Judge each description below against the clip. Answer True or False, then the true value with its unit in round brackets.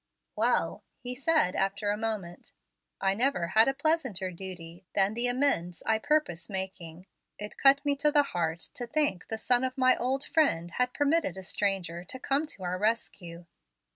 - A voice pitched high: True (215 Hz)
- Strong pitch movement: True (6.9 semitones)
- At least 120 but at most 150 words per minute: False (175 wpm)